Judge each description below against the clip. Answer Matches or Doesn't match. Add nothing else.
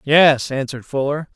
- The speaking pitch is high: Doesn't match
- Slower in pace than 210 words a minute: Matches